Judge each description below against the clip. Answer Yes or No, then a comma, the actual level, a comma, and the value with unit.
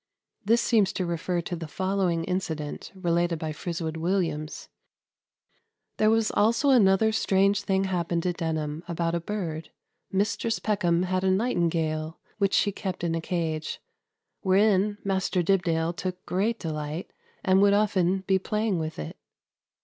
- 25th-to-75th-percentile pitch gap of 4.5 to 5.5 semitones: No, average, 3.1 semitones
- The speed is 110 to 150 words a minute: Yes, average, 145 wpm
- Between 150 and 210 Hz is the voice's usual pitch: Yes, medium, 185 Hz